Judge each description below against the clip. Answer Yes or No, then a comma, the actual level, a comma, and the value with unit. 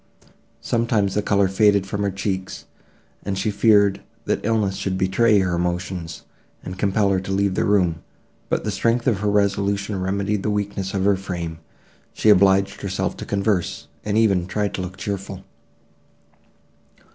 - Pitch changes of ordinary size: No, narrow, 1.5 semitones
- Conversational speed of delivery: Yes, average, 165 wpm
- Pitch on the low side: Yes, low, 100 Hz